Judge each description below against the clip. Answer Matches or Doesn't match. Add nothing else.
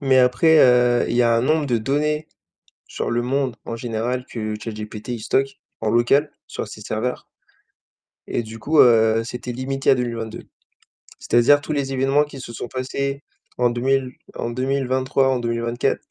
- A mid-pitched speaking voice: Doesn't match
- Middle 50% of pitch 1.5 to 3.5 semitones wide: Matches